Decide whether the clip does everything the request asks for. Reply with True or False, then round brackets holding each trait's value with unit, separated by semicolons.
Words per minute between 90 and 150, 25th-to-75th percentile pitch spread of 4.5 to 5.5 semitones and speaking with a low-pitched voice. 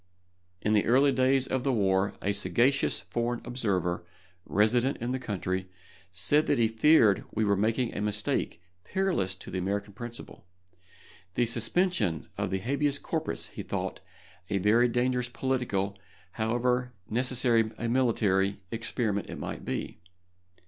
False (140 wpm; 3.9 semitones; 115 Hz)